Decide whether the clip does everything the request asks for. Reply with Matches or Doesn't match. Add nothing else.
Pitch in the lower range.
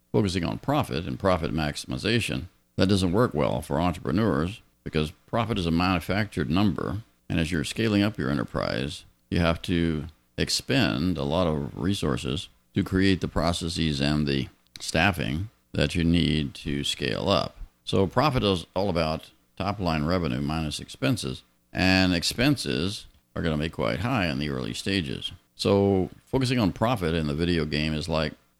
Matches